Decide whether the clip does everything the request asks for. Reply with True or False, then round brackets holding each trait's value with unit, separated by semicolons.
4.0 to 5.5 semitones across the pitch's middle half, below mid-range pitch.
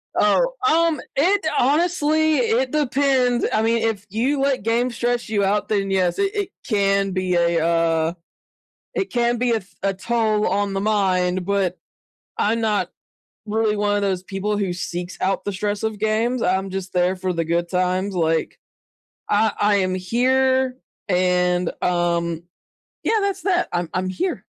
False (4.9 semitones; 205 Hz)